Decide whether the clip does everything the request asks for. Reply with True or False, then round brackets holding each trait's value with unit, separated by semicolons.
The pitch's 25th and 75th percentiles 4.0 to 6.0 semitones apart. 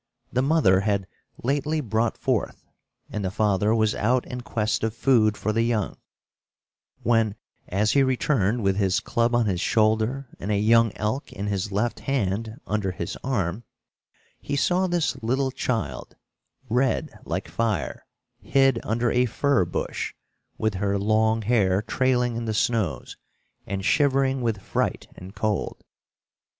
False (3.4 semitones)